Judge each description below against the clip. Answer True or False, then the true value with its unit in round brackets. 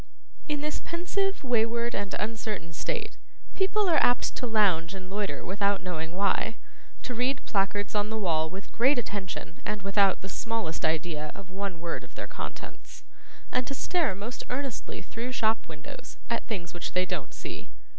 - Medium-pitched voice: False (205 Hz)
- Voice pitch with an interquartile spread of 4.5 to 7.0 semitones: True (4.9 semitones)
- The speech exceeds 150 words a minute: True (170 wpm)